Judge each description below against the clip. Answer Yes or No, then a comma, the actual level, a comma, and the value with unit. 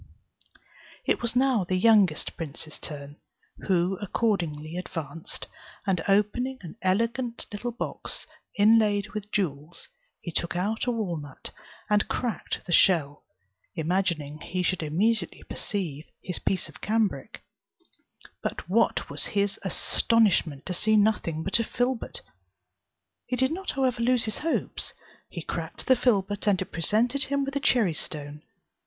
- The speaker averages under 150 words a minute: Yes, average, 140 wpm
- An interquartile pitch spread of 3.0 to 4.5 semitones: No, wide, 5.4 semitones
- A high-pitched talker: Yes, high, 200 Hz